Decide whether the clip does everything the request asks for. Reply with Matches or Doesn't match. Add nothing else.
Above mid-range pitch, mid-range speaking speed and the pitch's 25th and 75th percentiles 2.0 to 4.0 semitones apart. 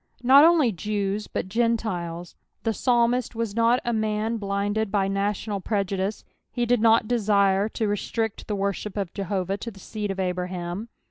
Matches